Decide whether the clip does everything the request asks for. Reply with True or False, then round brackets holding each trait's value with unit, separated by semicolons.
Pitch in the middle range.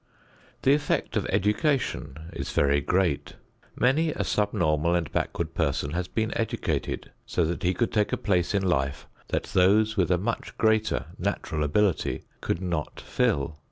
False (90 Hz)